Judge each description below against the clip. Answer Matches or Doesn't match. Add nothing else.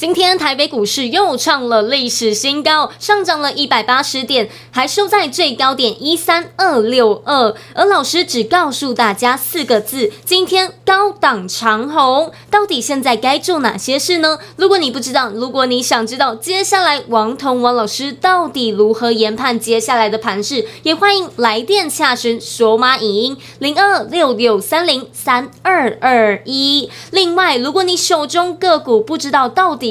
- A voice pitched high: Matches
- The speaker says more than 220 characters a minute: Matches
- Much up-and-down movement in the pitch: Matches